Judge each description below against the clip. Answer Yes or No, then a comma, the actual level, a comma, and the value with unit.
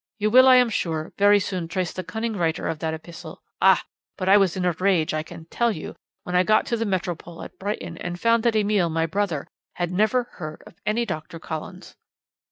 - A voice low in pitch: No, medium, 185 Hz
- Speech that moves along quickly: Yes, fast, 220 wpm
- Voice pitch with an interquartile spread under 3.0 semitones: No, average, 4.3 semitones